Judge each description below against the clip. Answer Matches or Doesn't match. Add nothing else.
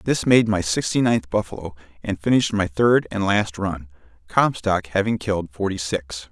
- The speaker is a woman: Doesn't match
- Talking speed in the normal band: Matches